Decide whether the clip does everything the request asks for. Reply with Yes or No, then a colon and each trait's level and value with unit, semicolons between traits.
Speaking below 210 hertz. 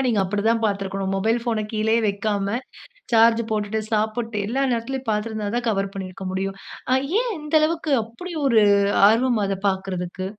No: high, 215 Hz